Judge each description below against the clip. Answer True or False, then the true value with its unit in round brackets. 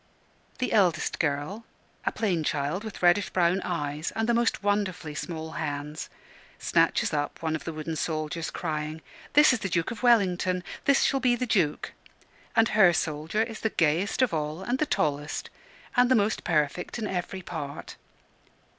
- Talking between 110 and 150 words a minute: False (170 wpm)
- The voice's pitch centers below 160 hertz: False (175 Hz)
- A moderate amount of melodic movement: False (5.8 semitones)